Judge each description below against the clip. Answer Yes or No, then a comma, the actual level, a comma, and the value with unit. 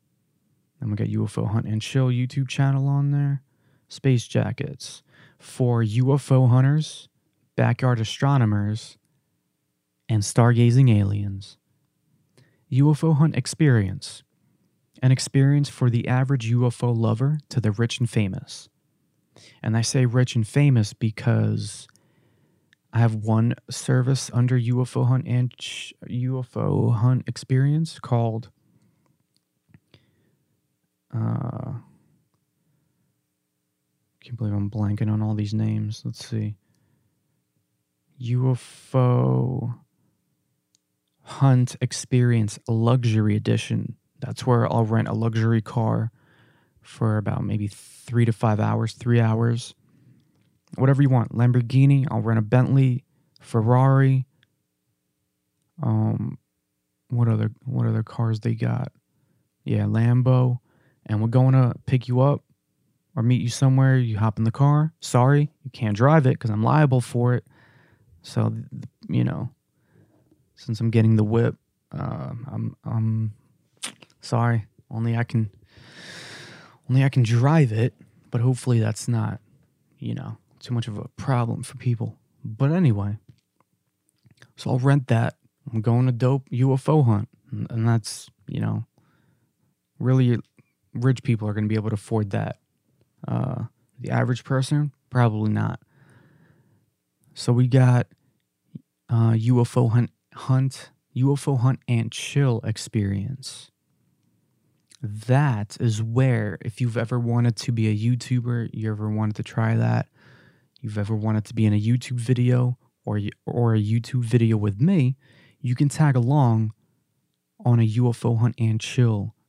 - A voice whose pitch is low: Yes, low, 120 Hz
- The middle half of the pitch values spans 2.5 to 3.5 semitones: Yes, average, 3.2 semitones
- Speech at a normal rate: No, slow, 130 wpm